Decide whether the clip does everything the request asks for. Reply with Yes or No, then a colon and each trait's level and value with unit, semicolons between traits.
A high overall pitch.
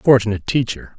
No: low, 115 Hz